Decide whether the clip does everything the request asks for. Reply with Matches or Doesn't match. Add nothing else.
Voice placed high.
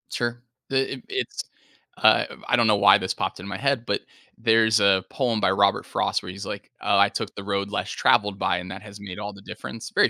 Doesn't match